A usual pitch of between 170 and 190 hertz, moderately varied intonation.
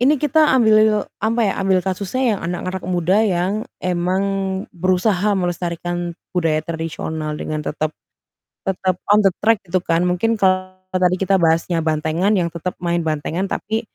Yes: medium, 185 Hz; average, 3.1 semitones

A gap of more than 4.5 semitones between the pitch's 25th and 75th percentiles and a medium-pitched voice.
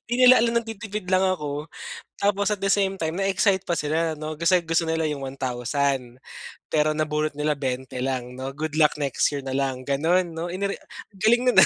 Yes: average, 5.2 semitones; medium, 155 Hz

